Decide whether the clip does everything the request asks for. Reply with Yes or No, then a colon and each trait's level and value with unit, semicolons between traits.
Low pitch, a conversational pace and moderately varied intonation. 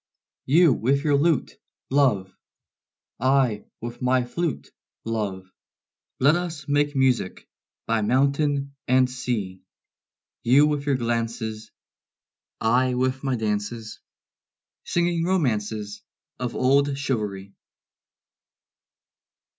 No: low, 130 Hz; slow, 95 wpm; average, 4.1 semitones